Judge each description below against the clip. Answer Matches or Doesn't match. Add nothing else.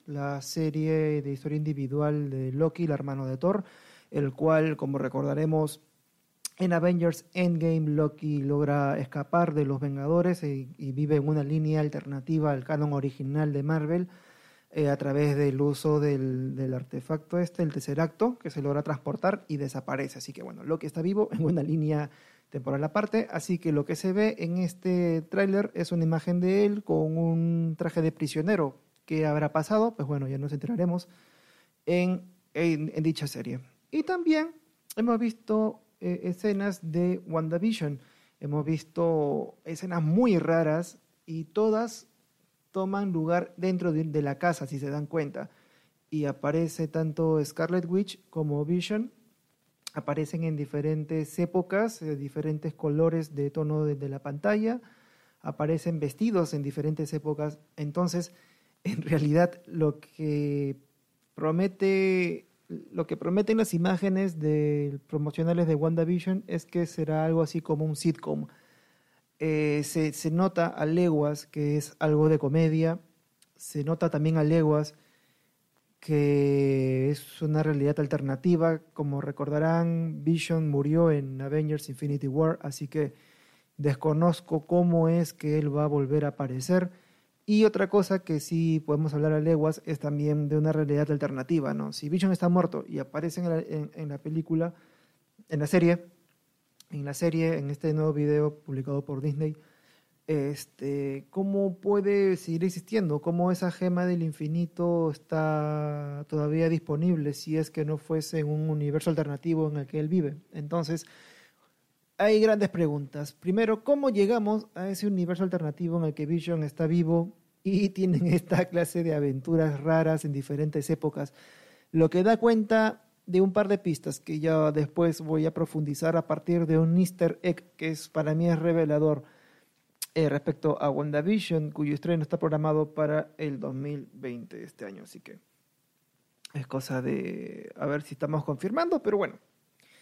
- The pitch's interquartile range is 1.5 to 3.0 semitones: Matches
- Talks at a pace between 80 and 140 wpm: Doesn't match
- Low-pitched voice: Doesn't match